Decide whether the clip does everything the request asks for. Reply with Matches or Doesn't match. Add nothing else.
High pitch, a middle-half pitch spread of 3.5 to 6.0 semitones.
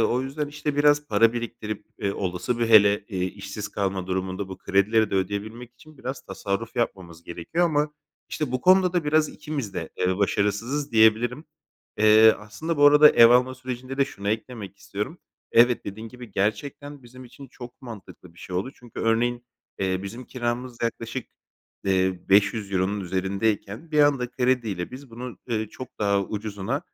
Doesn't match